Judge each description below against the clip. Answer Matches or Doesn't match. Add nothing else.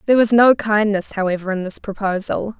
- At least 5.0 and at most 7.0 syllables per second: Matches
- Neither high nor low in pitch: Doesn't match